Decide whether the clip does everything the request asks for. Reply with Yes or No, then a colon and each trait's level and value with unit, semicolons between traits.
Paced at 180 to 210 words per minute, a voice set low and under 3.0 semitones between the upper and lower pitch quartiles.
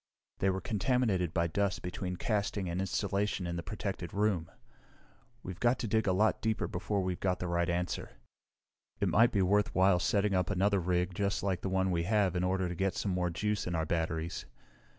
Yes: average, 200 wpm; very low, 95 Hz; narrow, 2.4 semitones